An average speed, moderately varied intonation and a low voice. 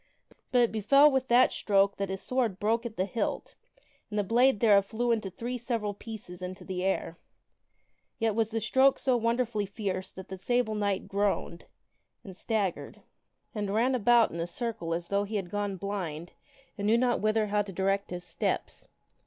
No: average, 185 wpm; average, 3.4 semitones; high, 210 Hz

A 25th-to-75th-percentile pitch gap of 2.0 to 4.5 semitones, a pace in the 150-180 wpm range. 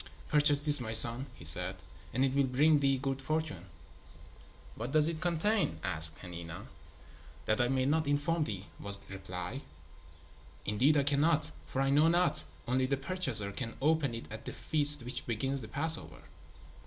No: average, 5.3 semitones; average, 170 wpm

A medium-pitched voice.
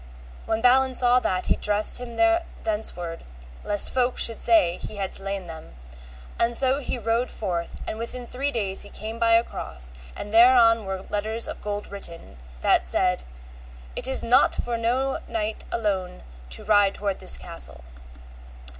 No: high, 220 Hz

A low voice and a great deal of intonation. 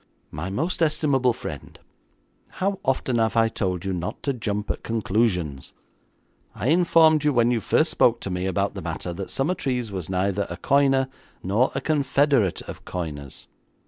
Yes: low, 115 Hz; wide, 6.7 semitones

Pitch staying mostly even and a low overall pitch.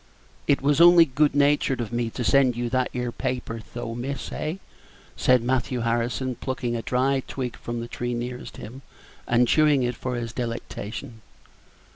Yes: narrow, 2.2 semitones; low, 125 Hz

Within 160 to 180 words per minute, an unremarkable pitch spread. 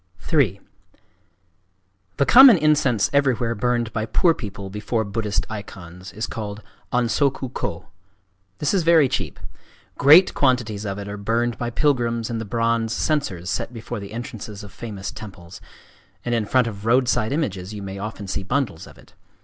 Yes: average, 165 wpm; average, 3.9 semitones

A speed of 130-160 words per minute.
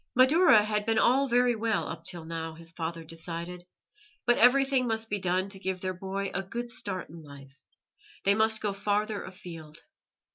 No: average, 180 wpm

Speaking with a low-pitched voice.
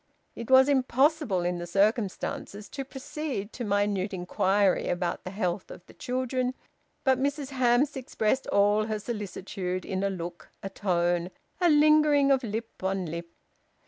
No: high, 210 Hz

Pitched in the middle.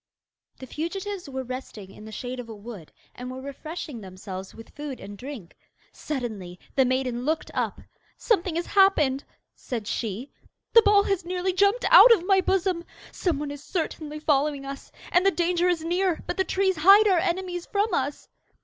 No: very high, 305 Hz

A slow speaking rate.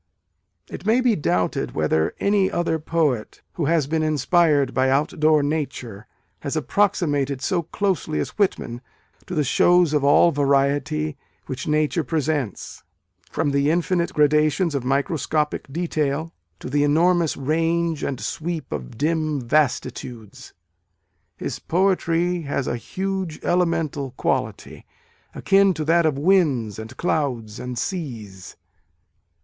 Yes: slow, 130 wpm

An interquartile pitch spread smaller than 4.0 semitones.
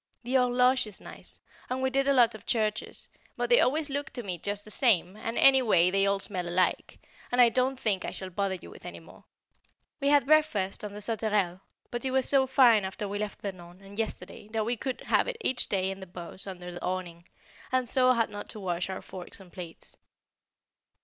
No: average, 5.2 semitones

